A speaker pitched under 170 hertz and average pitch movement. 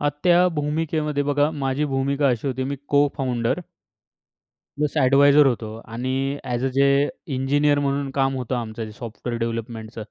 Yes: low, 135 Hz; average, 3.0 semitones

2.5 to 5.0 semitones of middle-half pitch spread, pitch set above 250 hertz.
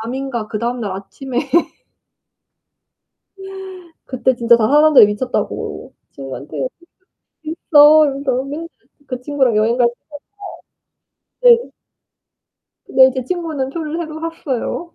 Yes: average, 4.5 semitones; very high, 265 Hz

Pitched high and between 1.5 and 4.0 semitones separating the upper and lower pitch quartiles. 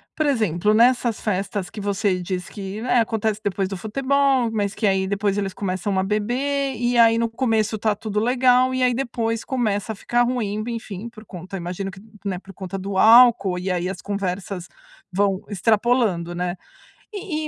Yes: high, 210 Hz; average, 3.7 semitones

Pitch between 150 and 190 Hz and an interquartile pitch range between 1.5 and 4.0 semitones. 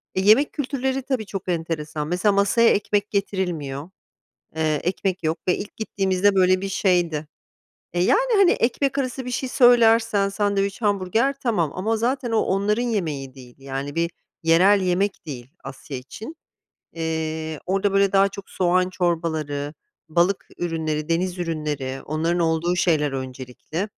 No: medium, 185 Hz; average, 4.6 semitones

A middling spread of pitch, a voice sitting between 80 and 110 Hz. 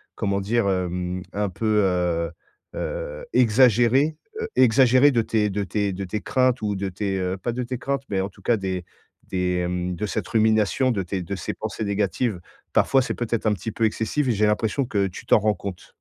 Yes: average, 4.1 semitones; low, 105 Hz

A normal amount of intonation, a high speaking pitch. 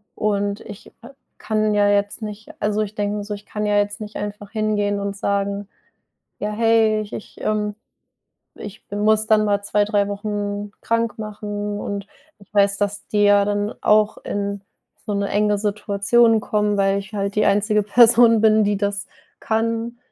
No: narrow, 0.9 semitones; high, 205 Hz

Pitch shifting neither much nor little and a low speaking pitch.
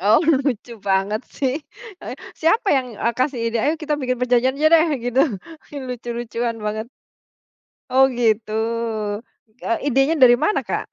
No: average, 3.1 semitones; very high, 250 Hz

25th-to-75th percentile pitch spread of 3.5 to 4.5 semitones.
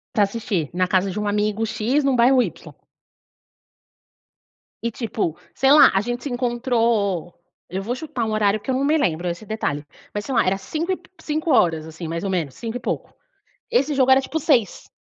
No: wide, 5.5 semitones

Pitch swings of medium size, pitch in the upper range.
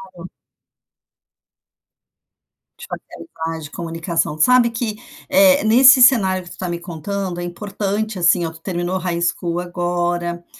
No: average, 3.5 semitones; medium, 175 Hz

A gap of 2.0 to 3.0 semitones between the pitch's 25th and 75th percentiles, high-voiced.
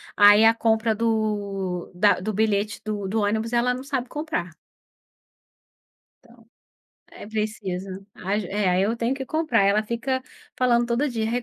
Yes: average, 2.7 semitones; high, 220 Hz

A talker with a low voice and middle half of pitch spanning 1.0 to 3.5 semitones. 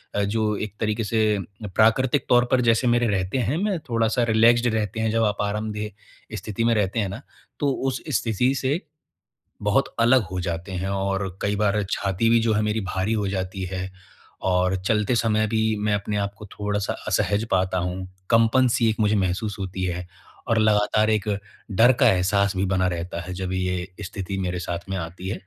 Yes: low, 105 Hz; average, 3.1 semitones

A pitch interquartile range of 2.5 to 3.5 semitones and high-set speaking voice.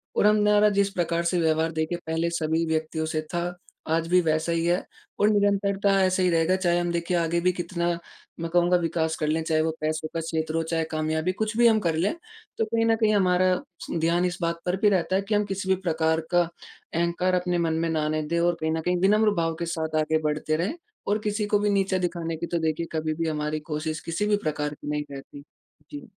No: average, 2.8 semitones; medium, 170 Hz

